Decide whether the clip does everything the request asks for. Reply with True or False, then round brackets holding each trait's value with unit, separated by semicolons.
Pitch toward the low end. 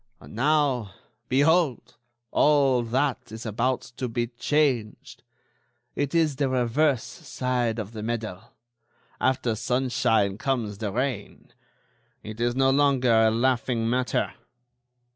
True (125 Hz)